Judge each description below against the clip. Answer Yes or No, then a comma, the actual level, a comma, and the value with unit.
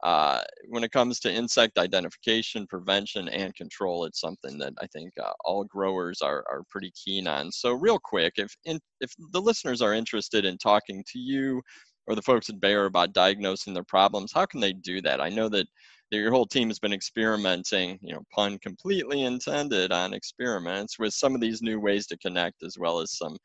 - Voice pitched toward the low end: Yes, low, 105 Hz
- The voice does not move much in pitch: No, average, 4.1 semitones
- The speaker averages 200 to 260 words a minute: Yes, fast, 205 wpm